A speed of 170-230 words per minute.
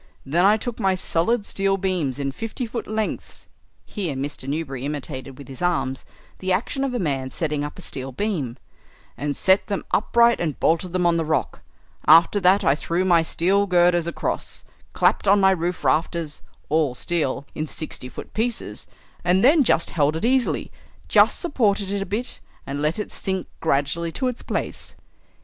Yes: average, 180 wpm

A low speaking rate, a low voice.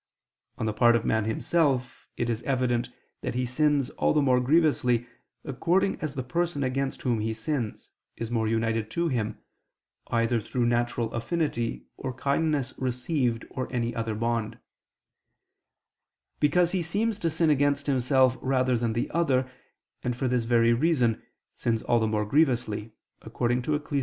No: average, 160 wpm; low, 125 Hz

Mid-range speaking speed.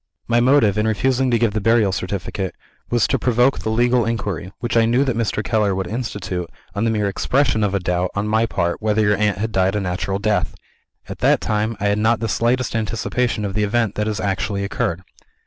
No: fast, 220 wpm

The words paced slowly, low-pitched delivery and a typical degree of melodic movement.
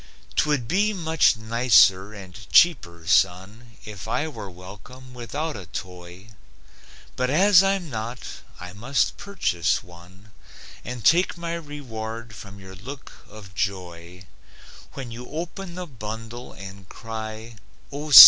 No: slow, 130 wpm; low, 115 Hz; wide, 7.2 semitones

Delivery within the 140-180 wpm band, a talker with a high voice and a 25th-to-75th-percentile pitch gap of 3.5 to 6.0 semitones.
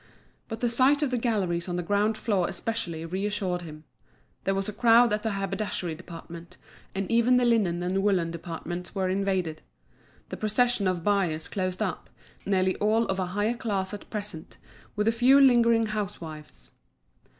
Yes: average, 170 wpm; high, 195 Hz; average, 4.1 semitones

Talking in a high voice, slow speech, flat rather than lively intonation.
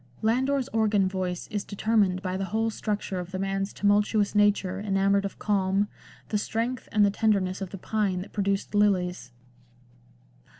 No: high, 200 Hz; average, 160 wpm; narrow, 1.9 semitones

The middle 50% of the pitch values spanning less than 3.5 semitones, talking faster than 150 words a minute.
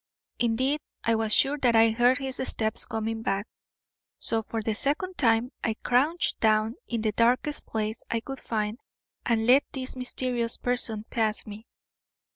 Yes: narrow, 2.5 semitones; average, 160 wpm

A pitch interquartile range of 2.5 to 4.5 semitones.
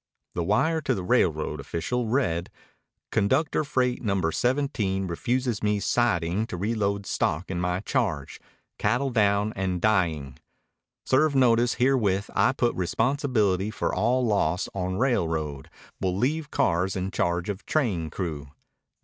No: wide, 5.6 semitones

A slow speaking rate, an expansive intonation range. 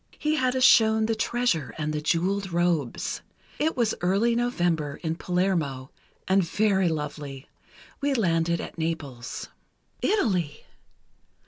Yes: slow, 125 wpm; wide, 5.9 semitones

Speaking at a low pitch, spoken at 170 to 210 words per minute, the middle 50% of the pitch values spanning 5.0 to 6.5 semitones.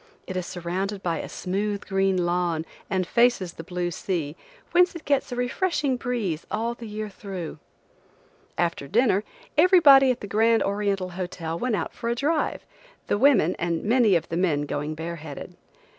No: high, 195 Hz; average, 175 wpm; wide, 5.6 semitones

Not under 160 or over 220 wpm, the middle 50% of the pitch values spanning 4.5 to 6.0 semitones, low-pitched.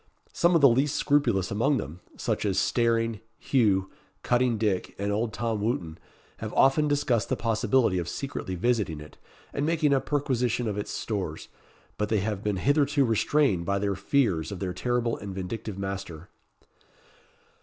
Yes: average, 165 wpm; average, 5.2 semitones; low, 110 Hz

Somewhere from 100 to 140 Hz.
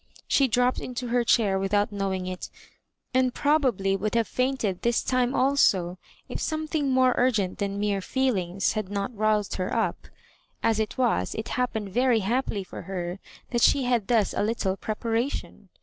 No: high, 220 Hz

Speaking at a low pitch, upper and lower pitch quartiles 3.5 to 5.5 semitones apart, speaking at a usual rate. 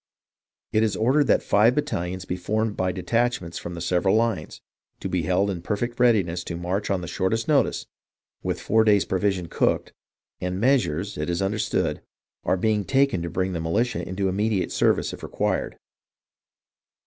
Yes: very low, 95 Hz; average, 3.9 semitones; average, 170 wpm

